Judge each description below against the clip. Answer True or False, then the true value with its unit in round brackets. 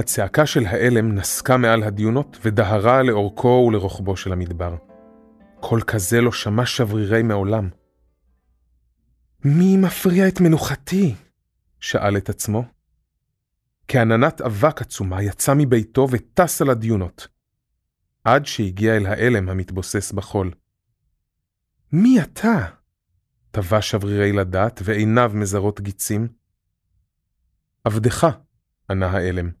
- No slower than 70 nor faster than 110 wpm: True (100 wpm)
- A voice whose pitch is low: True (110 Hz)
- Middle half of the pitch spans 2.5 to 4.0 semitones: False (4.5 semitones)